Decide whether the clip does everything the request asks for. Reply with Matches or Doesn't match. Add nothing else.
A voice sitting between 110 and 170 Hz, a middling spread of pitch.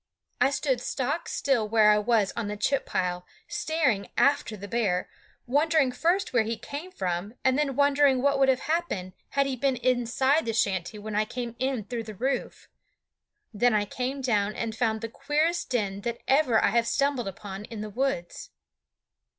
Doesn't match